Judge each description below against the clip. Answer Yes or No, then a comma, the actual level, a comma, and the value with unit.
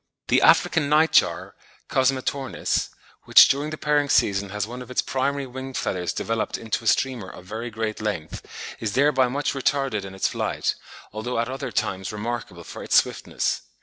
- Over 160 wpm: Yes, average, 175 wpm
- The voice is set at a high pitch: No, low, 120 Hz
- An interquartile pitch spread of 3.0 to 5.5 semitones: Yes, average, 4.3 semitones